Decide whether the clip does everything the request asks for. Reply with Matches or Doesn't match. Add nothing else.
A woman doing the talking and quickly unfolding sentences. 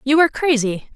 Doesn't match